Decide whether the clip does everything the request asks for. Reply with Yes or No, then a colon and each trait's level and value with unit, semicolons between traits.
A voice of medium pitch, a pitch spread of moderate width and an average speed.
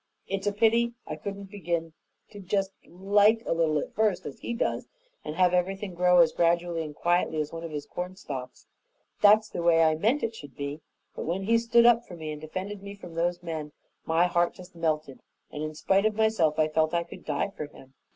No: medium, 175 Hz; average, 4.2 semitones; fast, 220 wpm